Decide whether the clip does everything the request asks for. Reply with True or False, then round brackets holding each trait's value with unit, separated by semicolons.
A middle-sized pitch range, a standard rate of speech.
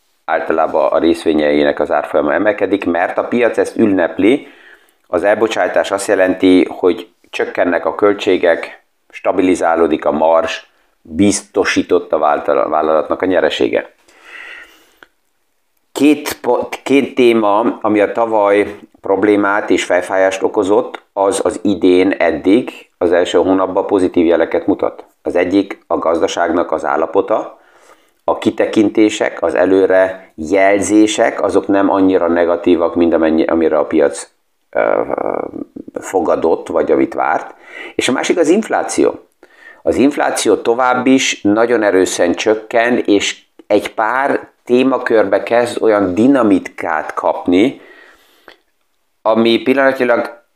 True (4.1 semitones; 115 wpm)